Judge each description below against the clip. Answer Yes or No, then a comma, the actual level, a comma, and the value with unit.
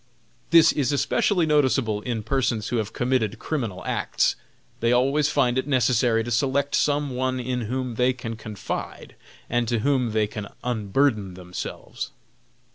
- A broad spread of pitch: No, average, 3.5 semitones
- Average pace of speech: Yes, average, 150 wpm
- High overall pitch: No, low, 125 Hz